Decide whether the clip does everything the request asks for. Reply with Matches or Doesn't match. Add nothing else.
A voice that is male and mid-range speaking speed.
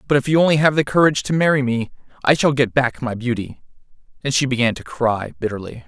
Doesn't match